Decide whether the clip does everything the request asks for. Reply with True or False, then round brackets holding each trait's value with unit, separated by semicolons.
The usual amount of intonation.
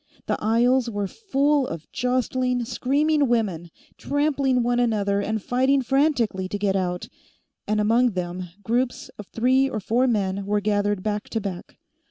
True (4.2 semitones)